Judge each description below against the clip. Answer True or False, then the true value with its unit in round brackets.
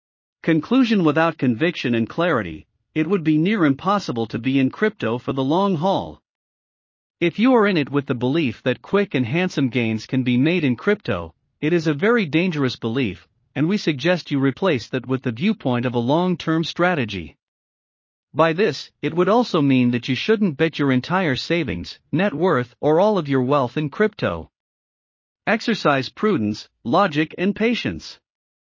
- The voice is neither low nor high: True (150 Hz)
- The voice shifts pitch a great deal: True (6.5 semitones)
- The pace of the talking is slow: False (170 wpm)